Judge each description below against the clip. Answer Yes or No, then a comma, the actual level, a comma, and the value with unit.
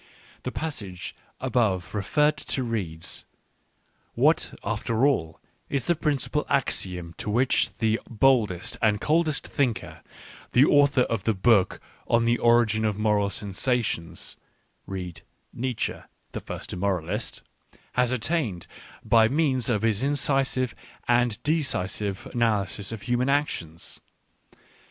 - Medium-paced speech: No, slow, 130 wpm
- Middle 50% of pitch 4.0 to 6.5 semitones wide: Yes, average, 4.9 semitones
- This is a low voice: Yes, low, 115 Hz